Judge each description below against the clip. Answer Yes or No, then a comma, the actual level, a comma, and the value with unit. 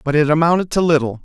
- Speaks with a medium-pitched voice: Yes, medium, 155 Hz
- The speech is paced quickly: Yes, fast, 240 wpm